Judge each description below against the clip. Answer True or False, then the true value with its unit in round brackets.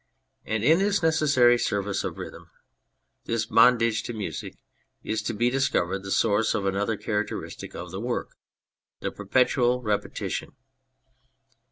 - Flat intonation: False (3.4 semitones)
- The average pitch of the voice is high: False (115 Hz)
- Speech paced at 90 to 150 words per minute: True (135 wpm)